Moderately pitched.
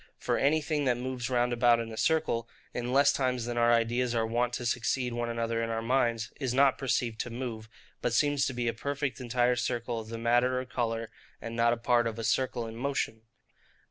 No: low, 120 Hz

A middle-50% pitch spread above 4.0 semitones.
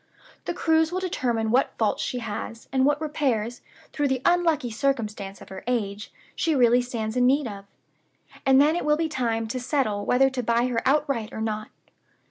Yes: average, 4.5 semitones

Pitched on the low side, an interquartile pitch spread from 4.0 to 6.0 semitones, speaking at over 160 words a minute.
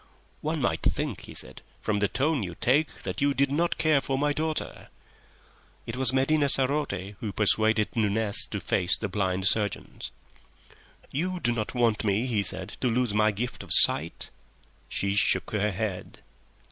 Yes: low, 110 Hz; average, 5.1 semitones; average, 170 wpm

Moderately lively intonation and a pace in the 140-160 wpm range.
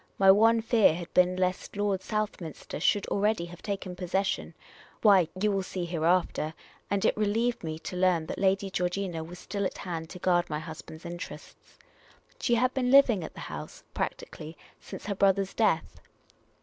No: average, 3.0 semitones; average, 180 wpm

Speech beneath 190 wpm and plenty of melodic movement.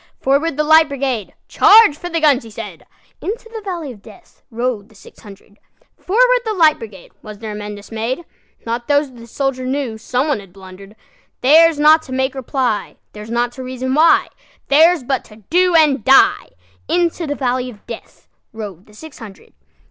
Yes: average, 150 wpm; wide, 6.0 semitones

